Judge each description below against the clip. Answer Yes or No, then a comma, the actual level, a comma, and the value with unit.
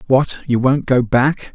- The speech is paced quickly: No, average, 195 wpm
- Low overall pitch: Yes, low, 130 Hz